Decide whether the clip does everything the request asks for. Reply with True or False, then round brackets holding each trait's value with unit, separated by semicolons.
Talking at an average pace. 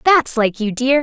False (235 wpm)